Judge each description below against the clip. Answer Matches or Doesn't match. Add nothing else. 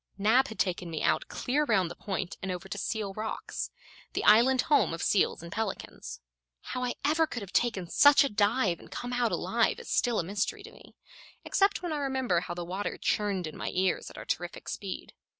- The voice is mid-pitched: Doesn't match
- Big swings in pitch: Matches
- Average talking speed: Doesn't match